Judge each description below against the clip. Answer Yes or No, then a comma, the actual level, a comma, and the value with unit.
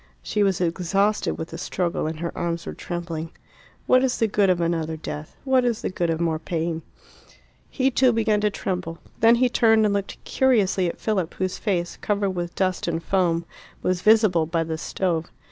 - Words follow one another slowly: No, average, 195 wpm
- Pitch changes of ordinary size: Yes, average, 4.1 semitones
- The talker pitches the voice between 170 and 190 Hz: Yes, medium, 185 Hz